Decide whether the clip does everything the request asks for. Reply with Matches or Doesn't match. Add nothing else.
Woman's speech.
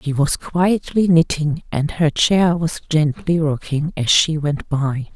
Matches